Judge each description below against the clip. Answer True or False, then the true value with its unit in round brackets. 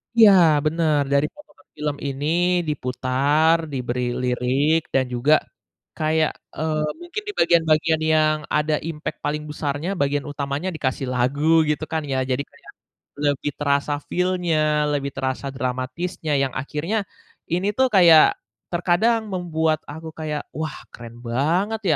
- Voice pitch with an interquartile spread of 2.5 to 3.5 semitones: True (2.9 semitones)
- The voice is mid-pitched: True (150 Hz)